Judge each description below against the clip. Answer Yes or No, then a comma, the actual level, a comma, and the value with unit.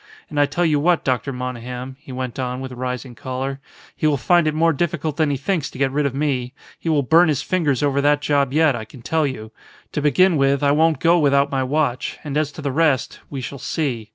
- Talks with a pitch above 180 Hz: No, medium, 140 Hz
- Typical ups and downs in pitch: Yes, average, 3.1 semitones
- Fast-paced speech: Yes, fast, 240 wpm